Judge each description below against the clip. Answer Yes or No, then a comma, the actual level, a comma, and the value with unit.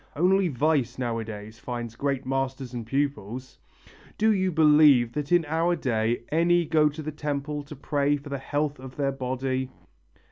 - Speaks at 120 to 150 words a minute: No, average, 165 wpm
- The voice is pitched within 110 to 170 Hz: Yes, medium, 140 Hz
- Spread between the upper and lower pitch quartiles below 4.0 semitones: Yes, average, 3.2 semitones